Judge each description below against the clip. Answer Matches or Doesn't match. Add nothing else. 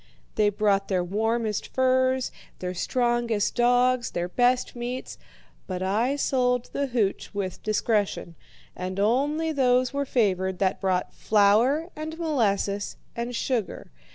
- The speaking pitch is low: Doesn't match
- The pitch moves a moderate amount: Matches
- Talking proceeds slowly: Matches